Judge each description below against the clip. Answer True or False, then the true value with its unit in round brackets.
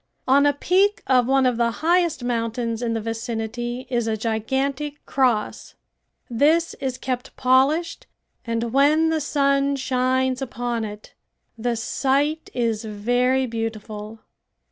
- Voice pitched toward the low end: False (250 Hz)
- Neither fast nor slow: False (130 wpm)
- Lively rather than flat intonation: False (3.3 semitones)